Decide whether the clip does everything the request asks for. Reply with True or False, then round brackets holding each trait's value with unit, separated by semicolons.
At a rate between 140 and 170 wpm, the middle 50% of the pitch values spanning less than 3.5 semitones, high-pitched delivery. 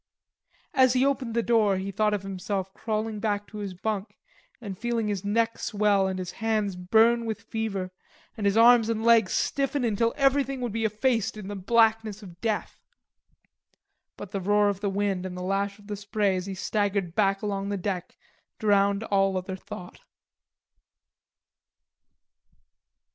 True (165 wpm; 2.4 semitones; 205 Hz)